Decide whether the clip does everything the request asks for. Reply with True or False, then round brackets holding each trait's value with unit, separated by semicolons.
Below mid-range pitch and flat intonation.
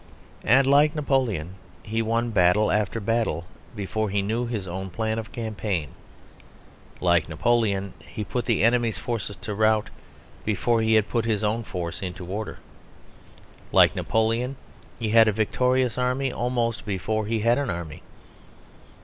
False (110 Hz; 3.1 semitones)